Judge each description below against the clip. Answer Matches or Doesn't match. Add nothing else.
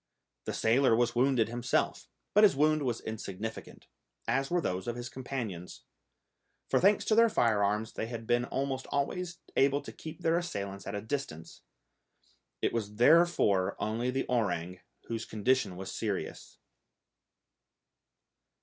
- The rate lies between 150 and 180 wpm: Doesn't match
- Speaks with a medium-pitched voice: Doesn't match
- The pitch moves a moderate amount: Matches